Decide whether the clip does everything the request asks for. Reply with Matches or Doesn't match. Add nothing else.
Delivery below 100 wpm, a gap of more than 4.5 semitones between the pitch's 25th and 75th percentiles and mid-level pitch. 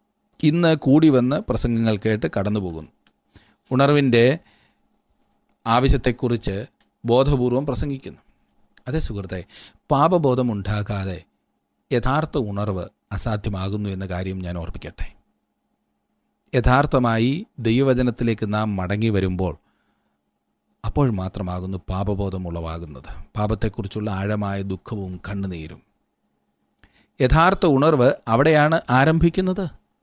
Doesn't match